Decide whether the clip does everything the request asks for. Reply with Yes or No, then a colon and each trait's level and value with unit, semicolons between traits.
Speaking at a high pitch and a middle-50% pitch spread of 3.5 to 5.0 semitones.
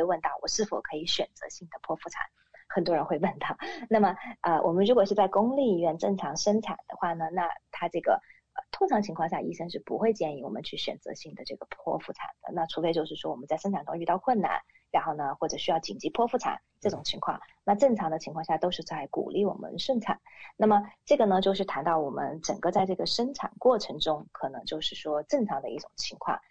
No: high, 195 Hz; wide, 5.5 semitones